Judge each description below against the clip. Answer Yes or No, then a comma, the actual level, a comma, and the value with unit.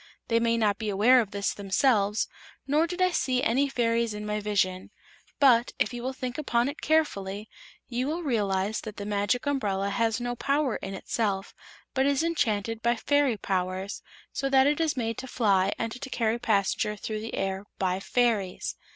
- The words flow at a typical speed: Yes, average, 185 wpm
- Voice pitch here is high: Yes, high, 230 Hz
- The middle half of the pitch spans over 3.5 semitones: Yes, average, 4.5 semitones